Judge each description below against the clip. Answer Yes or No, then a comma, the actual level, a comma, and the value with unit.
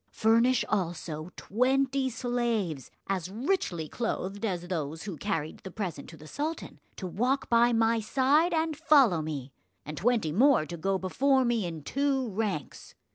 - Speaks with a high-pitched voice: Yes, high, 215 Hz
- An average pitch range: No, wide, 7.1 semitones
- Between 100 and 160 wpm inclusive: Yes, average, 155 wpm